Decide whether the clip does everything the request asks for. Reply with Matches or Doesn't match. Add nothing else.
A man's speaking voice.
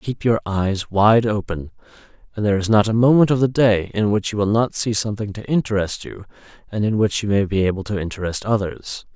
Matches